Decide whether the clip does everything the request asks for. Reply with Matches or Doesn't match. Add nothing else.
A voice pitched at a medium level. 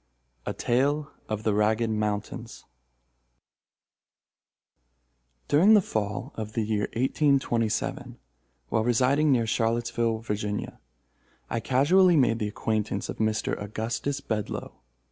Doesn't match